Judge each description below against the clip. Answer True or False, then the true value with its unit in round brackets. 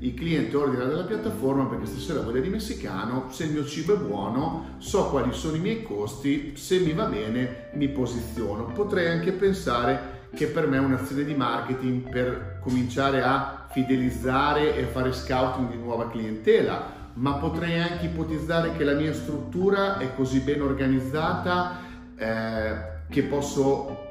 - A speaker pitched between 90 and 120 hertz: False (135 Hz)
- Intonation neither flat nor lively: True (3.6 semitones)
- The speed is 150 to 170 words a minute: True (155 wpm)